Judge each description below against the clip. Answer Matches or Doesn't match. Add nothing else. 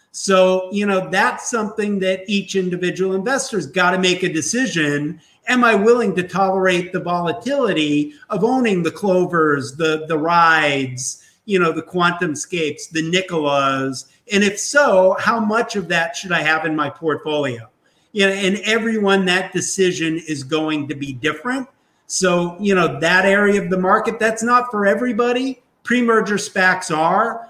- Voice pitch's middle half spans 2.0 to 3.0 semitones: Doesn't match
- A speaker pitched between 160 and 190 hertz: Matches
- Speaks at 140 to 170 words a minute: Matches